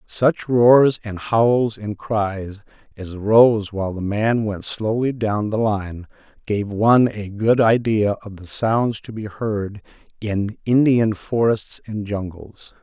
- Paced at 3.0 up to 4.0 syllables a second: Yes, 3.6 syllables/s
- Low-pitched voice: Yes, low, 105 Hz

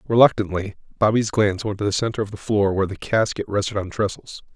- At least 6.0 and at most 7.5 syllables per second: Yes, 6.3 syllables/s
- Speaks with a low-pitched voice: Yes, low, 105 Hz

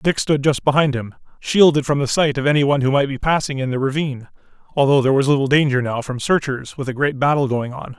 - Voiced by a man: Yes, male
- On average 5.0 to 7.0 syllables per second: Yes, 6.4 syllables/s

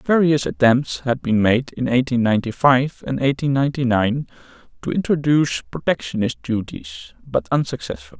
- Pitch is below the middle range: Yes, low, 125 Hz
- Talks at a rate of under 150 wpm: Yes, average, 140 wpm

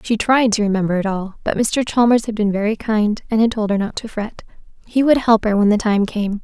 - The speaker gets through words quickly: Yes, fast, 260 wpm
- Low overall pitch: No, high, 215 Hz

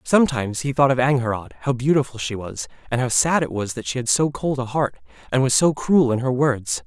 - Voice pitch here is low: Yes, low, 130 Hz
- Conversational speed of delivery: No, fast, 245 wpm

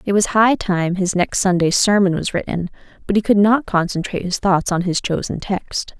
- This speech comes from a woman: Yes, female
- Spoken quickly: Yes, fast, 210 wpm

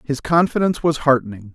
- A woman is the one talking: No, male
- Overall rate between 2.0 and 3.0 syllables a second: No, 6.2 syllables/s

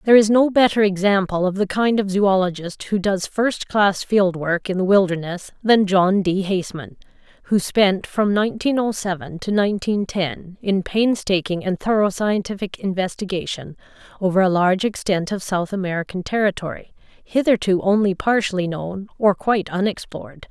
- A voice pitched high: Yes, high, 195 Hz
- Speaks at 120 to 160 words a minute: Yes, average, 155 wpm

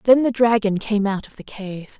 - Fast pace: Yes, fast, 240 wpm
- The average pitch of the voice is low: No, high, 215 Hz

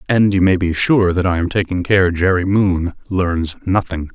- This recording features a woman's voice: No, male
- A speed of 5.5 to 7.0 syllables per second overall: No, 4.6 syllables/s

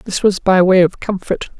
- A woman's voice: Yes, female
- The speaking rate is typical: No, fast, 225 wpm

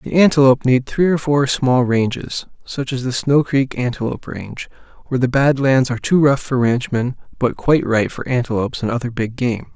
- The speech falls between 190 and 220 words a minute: Yes, fast, 205 wpm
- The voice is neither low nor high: No, low, 130 Hz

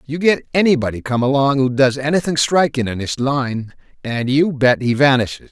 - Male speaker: Yes, male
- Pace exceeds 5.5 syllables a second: No, 5.2 syllables/s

